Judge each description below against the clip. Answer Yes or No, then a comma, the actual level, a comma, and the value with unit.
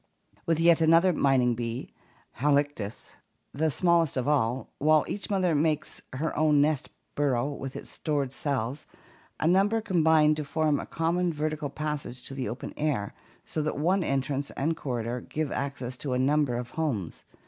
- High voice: No, medium, 145 Hz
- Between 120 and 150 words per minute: No, average, 165 wpm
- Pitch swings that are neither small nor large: Yes, average, 3.4 semitones